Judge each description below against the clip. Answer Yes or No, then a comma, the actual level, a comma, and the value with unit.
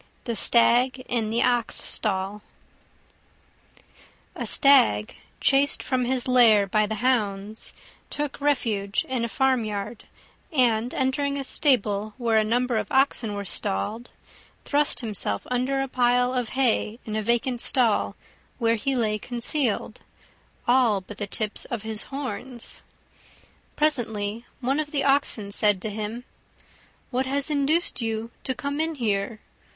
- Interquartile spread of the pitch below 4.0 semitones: Yes, average, 3.6 semitones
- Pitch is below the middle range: No, high, 240 Hz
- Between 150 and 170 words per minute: No, average, 140 wpm